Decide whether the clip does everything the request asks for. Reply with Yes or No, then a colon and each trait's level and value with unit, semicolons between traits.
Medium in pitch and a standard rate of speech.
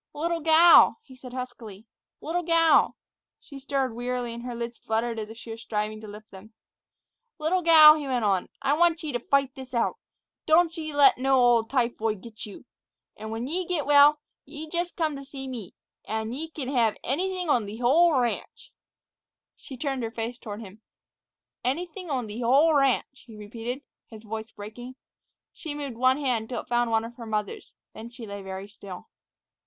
No: very high, 250 Hz; average, 190 wpm